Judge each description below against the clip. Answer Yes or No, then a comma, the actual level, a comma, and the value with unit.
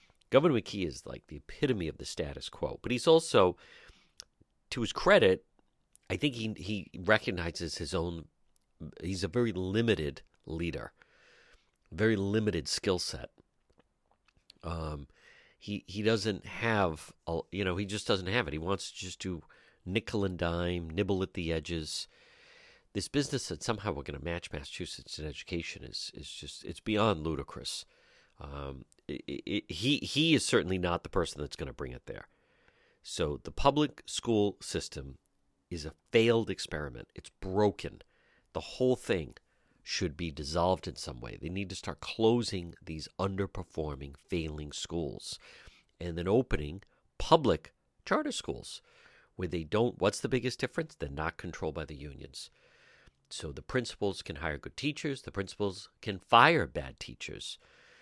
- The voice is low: Yes, very low, 95 Hz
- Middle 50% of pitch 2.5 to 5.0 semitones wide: No, wide, 5.4 semitones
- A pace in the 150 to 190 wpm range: Yes, average, 155 wpm